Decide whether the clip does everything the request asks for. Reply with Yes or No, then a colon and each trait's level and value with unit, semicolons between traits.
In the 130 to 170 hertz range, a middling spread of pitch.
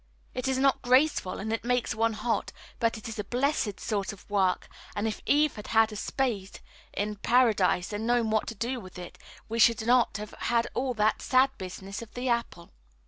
No: high, 225 Hz; average, 3.1 semitones